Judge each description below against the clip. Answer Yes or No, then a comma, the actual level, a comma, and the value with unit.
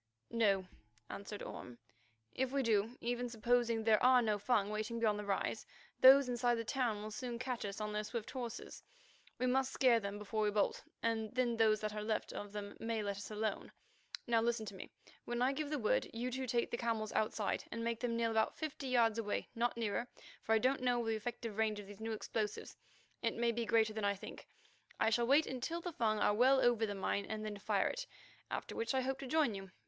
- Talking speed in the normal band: No, fast, 225 wpm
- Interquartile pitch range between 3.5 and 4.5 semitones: No, narrow, 2.5 semitones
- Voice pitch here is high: Yes, high, 230 Hz